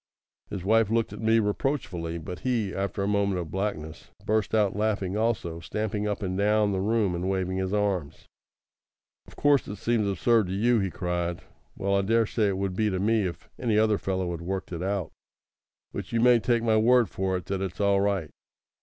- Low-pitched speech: Yes, low, 100 Hz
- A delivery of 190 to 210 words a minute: Yes, average, 200 wpm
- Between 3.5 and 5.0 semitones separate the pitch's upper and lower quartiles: No, average, 2.7 semitones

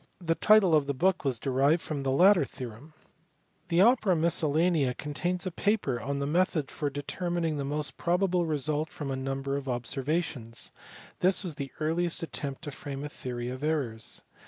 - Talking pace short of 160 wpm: No, average, 175 wpm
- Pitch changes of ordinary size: Yes, average, 4.1 semitones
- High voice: No, medium, 150 Hz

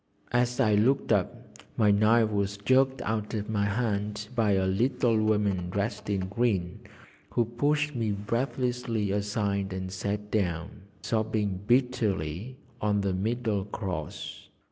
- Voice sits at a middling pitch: No, low, 105 Hz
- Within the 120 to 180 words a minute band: Yes, slow, 135 wpm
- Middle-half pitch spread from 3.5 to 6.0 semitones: No, average, 2.9 semitones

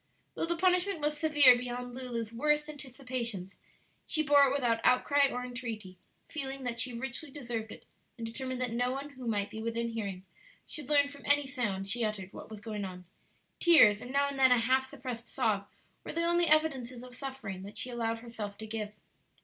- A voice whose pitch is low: No, very high, 250 Hz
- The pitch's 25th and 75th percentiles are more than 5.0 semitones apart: No, average, 3.9 semitones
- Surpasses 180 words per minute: Yes, average, 200 wpm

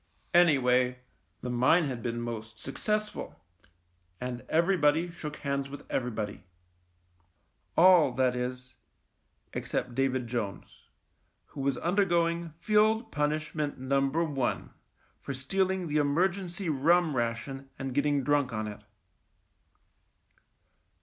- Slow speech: Yes, slow, 120 wpm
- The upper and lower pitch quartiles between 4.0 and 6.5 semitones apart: Yes, average, 5.2 semitones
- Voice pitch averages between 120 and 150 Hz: Yes, medium, 140 Hz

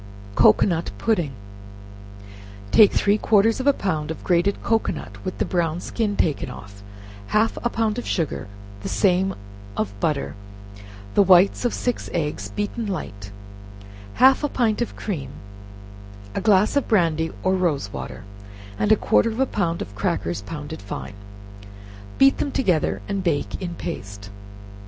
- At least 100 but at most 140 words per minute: No, average, 150 wpm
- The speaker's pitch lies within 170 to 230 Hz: Yes, medium, 185 Hz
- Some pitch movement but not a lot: No, wide, 6.3 semitones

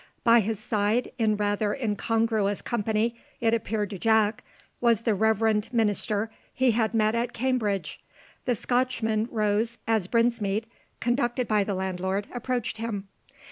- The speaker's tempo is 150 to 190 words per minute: No, average, 140 wpm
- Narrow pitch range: Yes, narrow, 2.2 semitones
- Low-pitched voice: No, high, 220 Hz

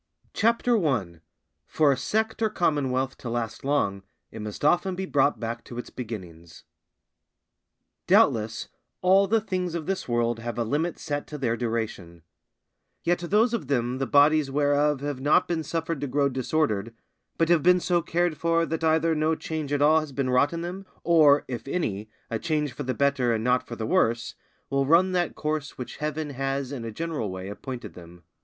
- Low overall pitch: No, medium, 145 Hz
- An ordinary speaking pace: Yes, average, 190 wpm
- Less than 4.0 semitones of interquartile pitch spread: No, wide, 5.6 semitones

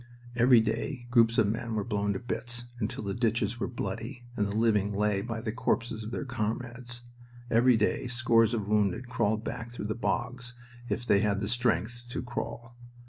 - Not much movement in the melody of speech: Yes, narrow, 2.3 semitones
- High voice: No, low, 115 Hz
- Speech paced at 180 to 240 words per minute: Yes, average, 190 wpm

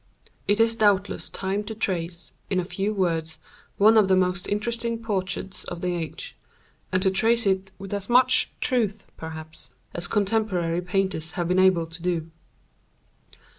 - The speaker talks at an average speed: Yes, average, 160 wpm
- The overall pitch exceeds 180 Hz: Yes, high, 190 Hz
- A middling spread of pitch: Yes, average, 3.1 semitones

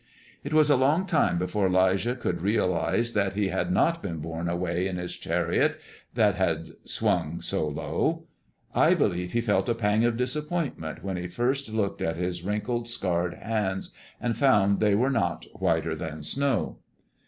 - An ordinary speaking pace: Yes, average, 170 wpm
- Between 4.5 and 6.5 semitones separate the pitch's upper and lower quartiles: Yes, average, 5.2 semitones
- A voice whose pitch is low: Yes, low, 100 Hz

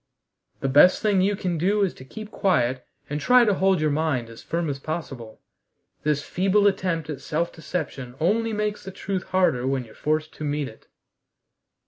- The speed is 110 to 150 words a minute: No, average, 185 wpm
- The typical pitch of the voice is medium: Yes, medium, 160 Hz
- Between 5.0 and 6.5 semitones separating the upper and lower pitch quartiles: Yes, wide, 5.5 semitones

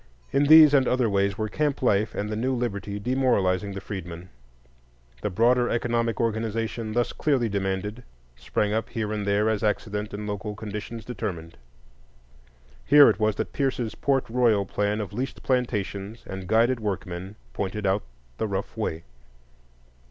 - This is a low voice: Yes, low, 105 Hz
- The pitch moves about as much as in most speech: Yes, average, 3.2 semitones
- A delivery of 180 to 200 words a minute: No, average, 155 wpm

